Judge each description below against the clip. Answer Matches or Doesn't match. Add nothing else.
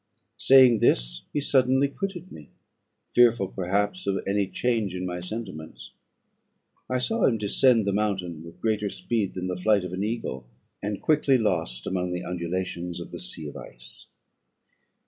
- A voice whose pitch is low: Matches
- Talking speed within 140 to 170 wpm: Matches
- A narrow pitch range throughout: Doesn't match